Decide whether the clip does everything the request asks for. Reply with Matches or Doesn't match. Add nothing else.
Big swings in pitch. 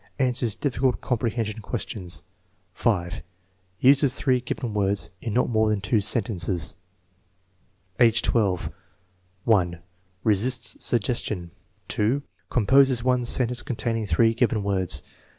Doesn't match